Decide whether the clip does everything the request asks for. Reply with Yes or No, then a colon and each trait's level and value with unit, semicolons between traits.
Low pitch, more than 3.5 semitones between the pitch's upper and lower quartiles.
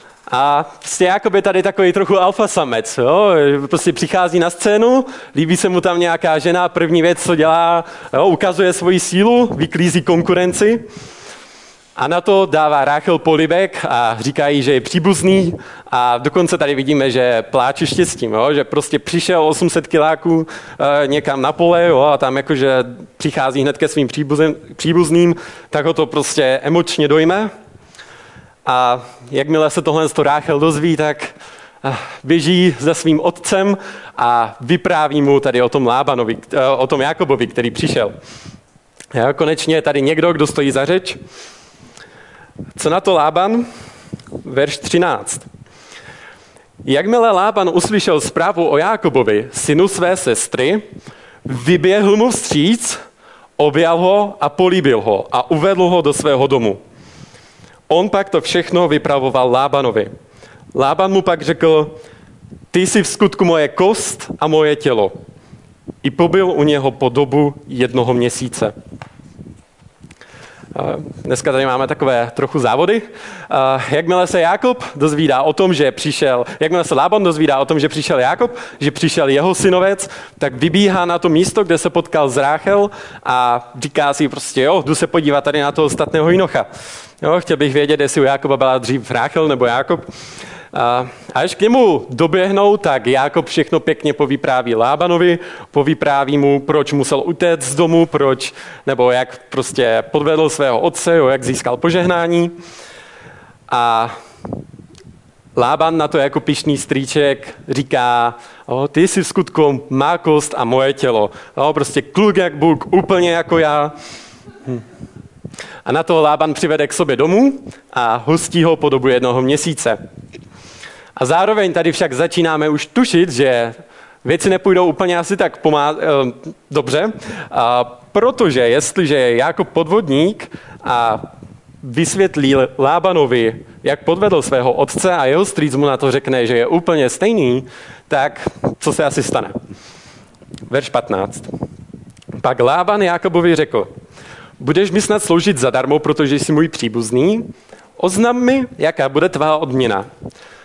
No: medium, 155 Hz; average, 4.3 semitones